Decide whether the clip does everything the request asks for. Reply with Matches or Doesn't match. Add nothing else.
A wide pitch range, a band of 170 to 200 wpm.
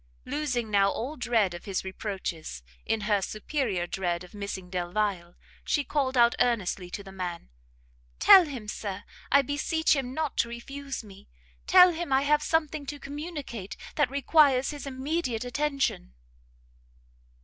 Doesn't match